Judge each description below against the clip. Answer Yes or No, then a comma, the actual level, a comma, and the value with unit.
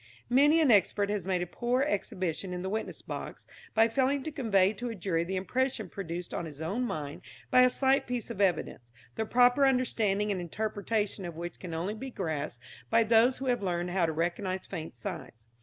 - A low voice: No, high, 200 Hz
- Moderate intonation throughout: No, wide, 5.8 semitones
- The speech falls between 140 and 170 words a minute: No, fast, 205 wpm